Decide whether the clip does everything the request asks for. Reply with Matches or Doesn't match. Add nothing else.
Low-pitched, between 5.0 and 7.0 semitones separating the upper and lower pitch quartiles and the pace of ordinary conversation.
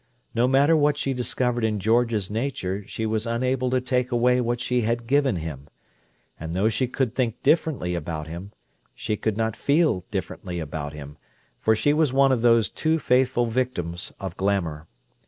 Matches